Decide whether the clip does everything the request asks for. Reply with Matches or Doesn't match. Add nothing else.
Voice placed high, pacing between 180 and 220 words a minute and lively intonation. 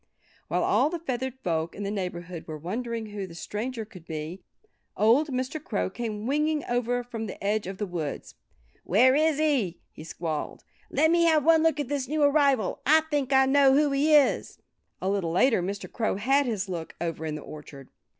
Matches